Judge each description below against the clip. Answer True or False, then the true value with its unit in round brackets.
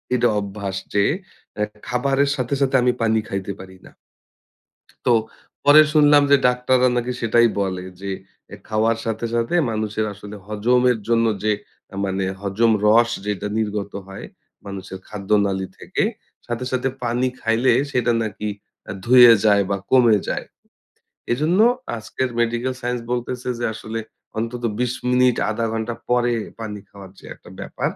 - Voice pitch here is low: True (115 Hz)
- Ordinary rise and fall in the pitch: True (3.1 semitones)